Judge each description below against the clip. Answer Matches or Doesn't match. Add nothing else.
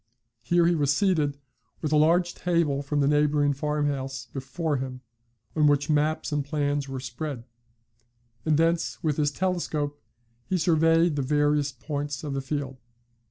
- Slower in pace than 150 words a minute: Doesn't match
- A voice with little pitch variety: Matches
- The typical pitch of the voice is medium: Matches